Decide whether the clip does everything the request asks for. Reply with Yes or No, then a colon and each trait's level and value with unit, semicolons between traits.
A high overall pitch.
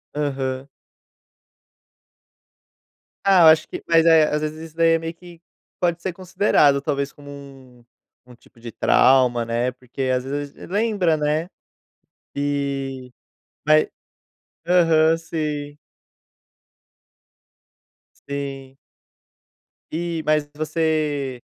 No: medium, 150 Hz